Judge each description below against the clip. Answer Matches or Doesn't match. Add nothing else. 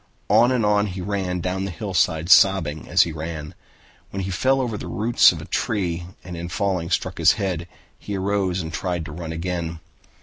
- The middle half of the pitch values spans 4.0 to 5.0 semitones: Doesn't match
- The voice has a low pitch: Matches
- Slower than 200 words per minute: Doesn't match